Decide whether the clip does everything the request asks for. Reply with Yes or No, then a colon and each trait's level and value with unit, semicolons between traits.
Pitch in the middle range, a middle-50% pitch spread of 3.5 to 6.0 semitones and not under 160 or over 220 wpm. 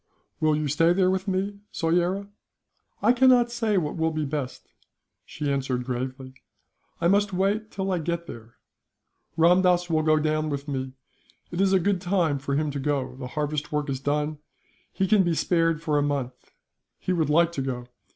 Yes: medium, 155 Hz; average, 4.4 semitones; average, 185 wpm